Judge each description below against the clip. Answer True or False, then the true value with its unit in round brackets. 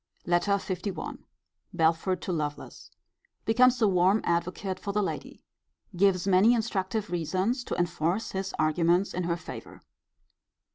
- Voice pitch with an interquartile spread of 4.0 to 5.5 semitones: False (2.7 semitones)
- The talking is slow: True (130 wpm)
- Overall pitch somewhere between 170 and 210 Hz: True (185 Hz)